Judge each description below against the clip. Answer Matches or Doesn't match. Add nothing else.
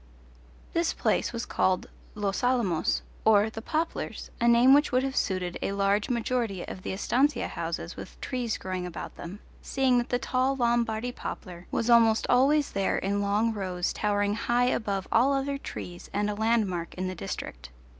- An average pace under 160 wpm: Doesn't match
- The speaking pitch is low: Doesn't match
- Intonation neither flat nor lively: Matches